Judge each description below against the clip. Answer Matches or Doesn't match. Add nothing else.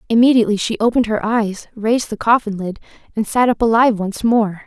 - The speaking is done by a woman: Matches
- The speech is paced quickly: Doesn't match